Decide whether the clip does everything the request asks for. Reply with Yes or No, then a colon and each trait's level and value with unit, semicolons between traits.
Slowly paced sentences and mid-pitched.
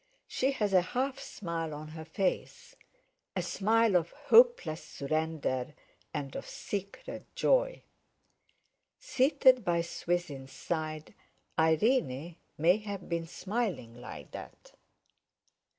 Yes: slow, 105 wpm; medium, 175 Hz